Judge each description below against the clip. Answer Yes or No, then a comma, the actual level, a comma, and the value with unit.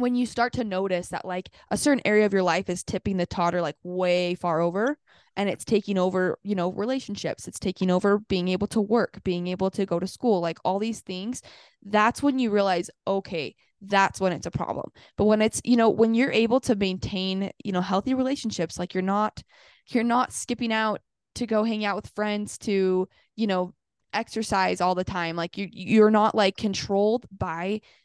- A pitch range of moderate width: Yes, average, 3.2 semitones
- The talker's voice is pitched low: No, high, 200 Hz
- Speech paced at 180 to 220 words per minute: Yes, fast, 205 wpm